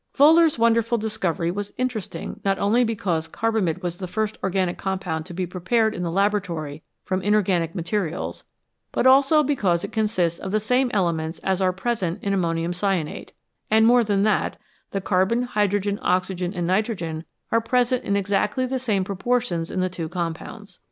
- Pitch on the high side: Yes, high, 195 Hz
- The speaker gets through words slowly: No, average, 170 wpm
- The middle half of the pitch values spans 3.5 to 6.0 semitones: Yes, average, 4.0 semitones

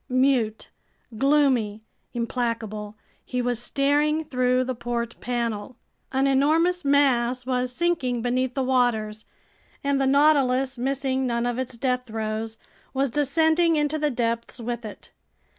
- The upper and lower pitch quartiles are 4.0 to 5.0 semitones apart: No, average, 2.8 semitones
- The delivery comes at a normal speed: No, slow, 130 wpm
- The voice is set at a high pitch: Yes, very high, 255 Hz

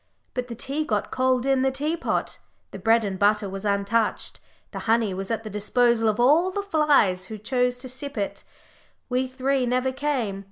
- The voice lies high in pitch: Yes, high, 245 Hz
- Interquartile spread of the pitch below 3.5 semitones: No, average, 4.0 semitones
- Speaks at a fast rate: No, average, 190 wpm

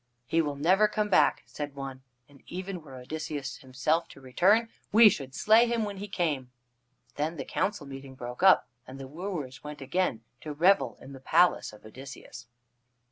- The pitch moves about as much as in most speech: No, wide, 5.9 semitones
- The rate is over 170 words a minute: Yes, average, 180 wpm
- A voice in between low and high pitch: Yes, medium, 150 Hz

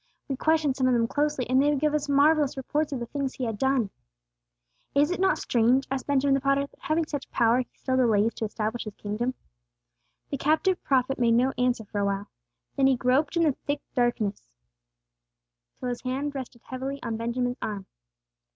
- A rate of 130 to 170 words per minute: No, average, 195 wpm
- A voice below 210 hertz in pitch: No, very high, 260 Hz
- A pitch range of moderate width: Yes, average, 3.1 semitones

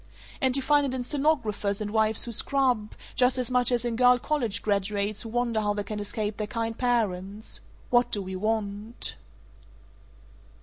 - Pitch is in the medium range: No, high, 225 Hz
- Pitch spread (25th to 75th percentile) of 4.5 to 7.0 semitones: No, average, 3.2 semitones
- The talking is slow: No, average, 175 wpm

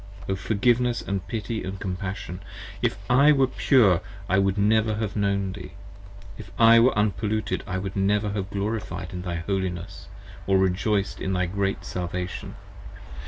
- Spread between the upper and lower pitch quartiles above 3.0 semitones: No, average, 2.7 semitones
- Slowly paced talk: No, average, 150 wpm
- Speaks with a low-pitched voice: Yes, low, 100 Hz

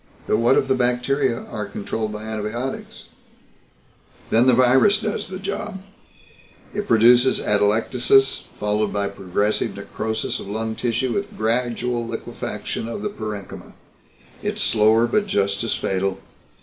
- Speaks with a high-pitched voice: No, low, 115 Hz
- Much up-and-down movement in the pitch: No, average, 3.6 semitones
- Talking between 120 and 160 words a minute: Yes, slow, 135 wpm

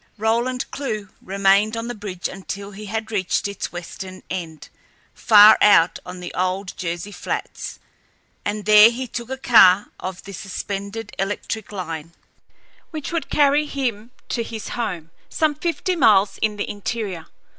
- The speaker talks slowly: No, average, 150 wpm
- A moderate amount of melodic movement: Yes, average, 3.5 semitones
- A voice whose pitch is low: No, high, 205 Hz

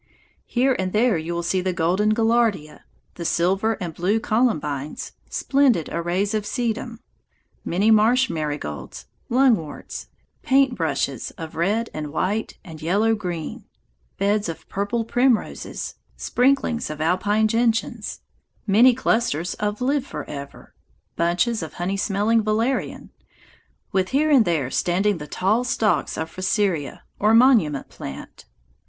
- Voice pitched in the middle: No, high, 205 Hz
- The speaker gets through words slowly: Yes, slow, 130 wpm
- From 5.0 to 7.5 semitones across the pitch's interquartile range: Yes, wide, 5.4 semitones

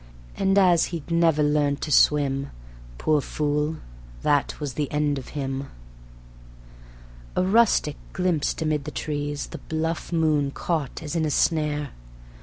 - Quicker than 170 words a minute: No, average, 140 wpm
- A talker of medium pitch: Yes, medium, 150 Hz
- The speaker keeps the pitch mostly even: Yes, narrow, 2.0 semitones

